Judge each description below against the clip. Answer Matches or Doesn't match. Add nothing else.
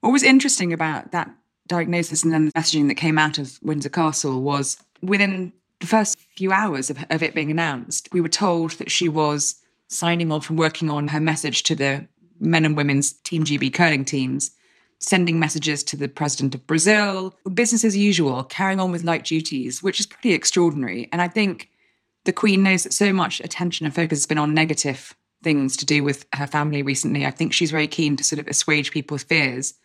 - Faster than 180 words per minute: Matches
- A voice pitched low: Doesn't match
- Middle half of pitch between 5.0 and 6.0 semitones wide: Doesn't match